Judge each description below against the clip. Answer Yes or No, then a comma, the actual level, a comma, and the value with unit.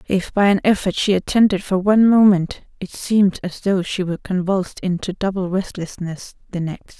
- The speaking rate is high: No, average, 180 wpm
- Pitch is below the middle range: No, high, 190 Hz